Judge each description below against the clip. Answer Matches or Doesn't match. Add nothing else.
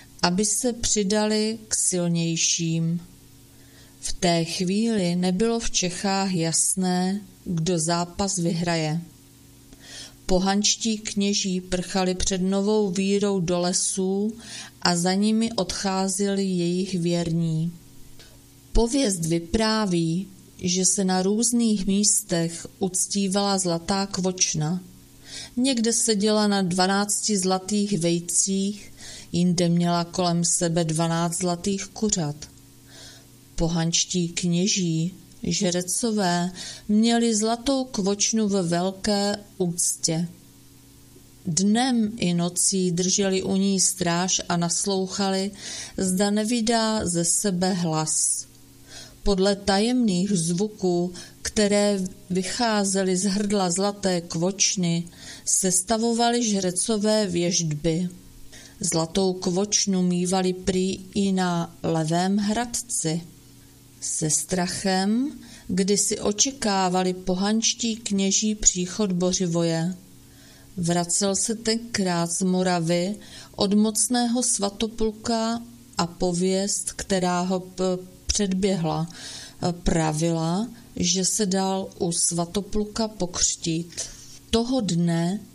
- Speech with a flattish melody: Doesn't match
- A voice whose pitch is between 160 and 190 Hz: Matches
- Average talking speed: Doesn't match